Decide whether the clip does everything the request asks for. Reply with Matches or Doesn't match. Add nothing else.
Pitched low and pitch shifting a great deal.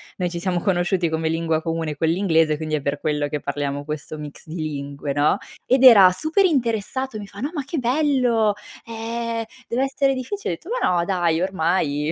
Doesn't match